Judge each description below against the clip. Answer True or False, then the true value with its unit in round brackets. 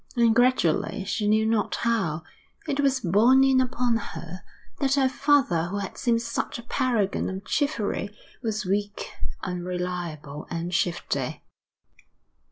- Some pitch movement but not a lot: False (5.7 semitones)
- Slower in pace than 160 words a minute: True (135 wpm)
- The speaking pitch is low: False (215 Hz)